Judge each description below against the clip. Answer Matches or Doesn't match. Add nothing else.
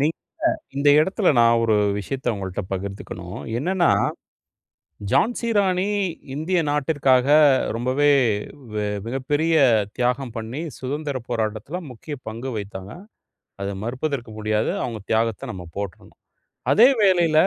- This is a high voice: Doesn't match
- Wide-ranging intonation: Matches